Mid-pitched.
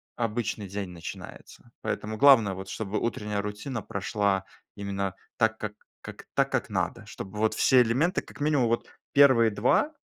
No: low, 110 Hz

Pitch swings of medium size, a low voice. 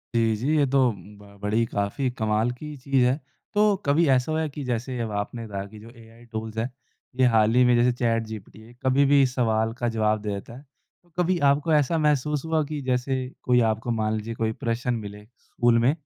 Yes: average, 3.7 semitones; low, 120 Hz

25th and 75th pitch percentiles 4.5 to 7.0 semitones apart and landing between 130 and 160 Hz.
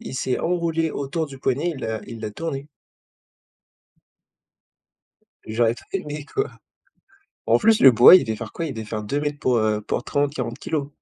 Yes: wide, 5.6 semitones; medium, 140 Hz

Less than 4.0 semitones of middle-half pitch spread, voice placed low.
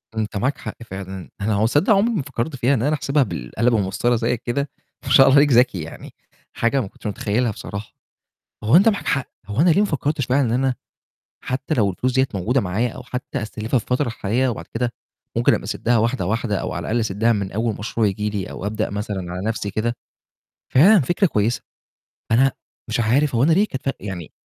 No: average, 4.4 semitones; low, 115 Hz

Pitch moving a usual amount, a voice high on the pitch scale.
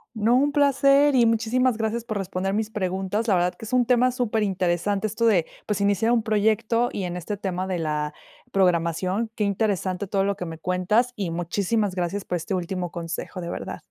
Yes: average, 3.8 semitones; high, 200 Hz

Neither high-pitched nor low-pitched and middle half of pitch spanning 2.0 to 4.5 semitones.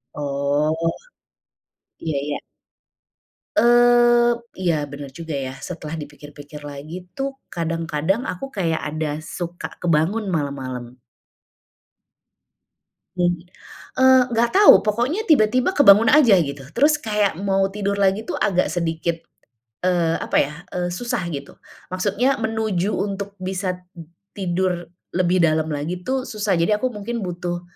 No: medium, 180 Hz; average, 5.2 semitones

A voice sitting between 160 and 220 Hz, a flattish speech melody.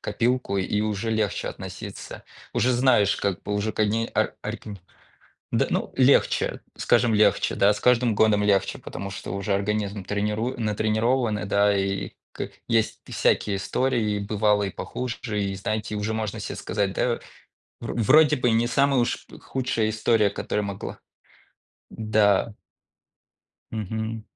No: low, 110 Hz; narrow, 2.2 semitones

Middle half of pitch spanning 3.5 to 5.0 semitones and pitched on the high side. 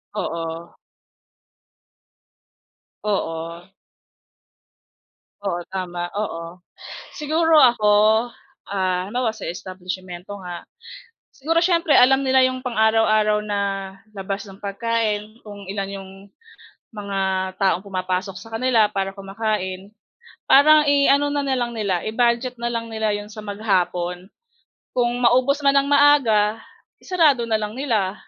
Yes: average, 4.5 semitones; high, 215 Hz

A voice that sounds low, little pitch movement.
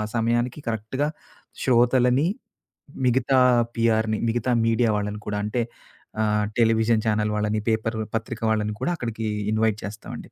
Yes: low, 110 Hz; narrow, 1.9 semitones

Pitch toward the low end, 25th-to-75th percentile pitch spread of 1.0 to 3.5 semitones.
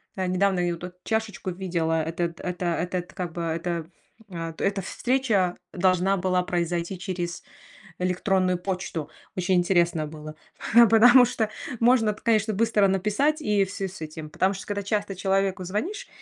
No: medium, 185 Hz; average, 2.9 semitones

